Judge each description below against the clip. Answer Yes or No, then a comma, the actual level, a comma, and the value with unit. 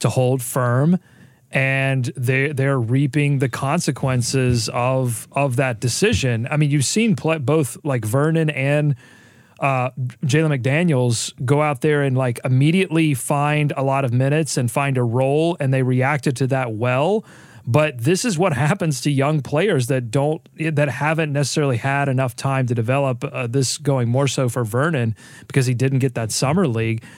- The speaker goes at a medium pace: Yes, average, 170 wpm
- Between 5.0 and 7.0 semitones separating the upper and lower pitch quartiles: No, average, 2.8 semitones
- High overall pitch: No, low, 135 Hz